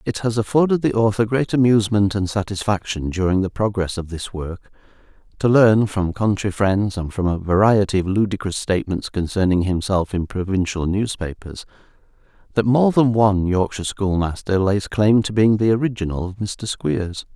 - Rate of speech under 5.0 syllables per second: No, 5.1 syllables/s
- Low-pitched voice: Yes, low, 100 Hz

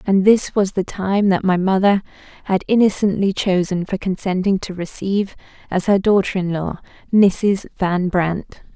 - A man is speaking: No, female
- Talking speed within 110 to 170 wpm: Yes, average, 160 wpm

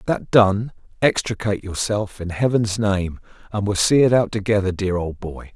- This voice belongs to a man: Yes, male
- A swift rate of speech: No, average, 175 wpm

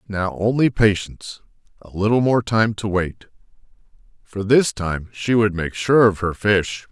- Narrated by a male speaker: Yes, male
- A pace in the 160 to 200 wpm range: Yes, average, 165 wpm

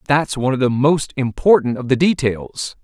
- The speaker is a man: Yes, male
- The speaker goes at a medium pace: Yes, average, 190 wpm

